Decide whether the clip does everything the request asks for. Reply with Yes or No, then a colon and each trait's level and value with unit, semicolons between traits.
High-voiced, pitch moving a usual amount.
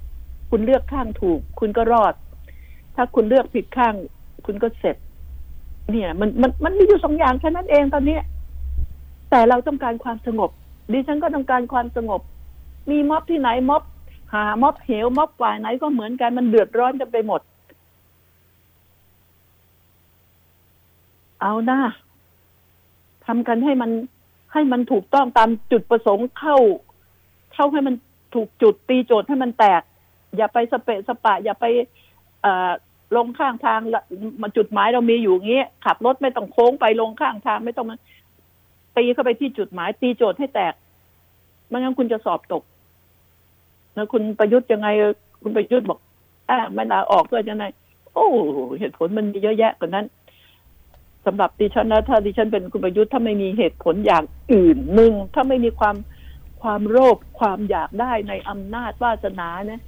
No: high, 225 Hz; wide, 7.0 semitones